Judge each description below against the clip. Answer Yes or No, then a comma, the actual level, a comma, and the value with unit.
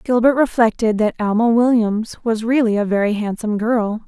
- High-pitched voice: Yes, high, 225 Hz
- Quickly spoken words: No, average, 160 wpm